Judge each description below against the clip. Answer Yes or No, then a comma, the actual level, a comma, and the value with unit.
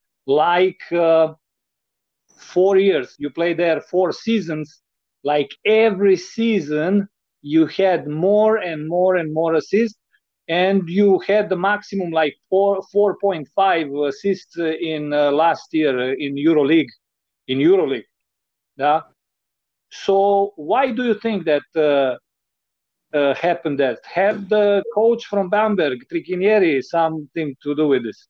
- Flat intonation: No, average, 4.7 semitones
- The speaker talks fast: No, average, 125 wpm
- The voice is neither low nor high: Yes, medium, 180 Hz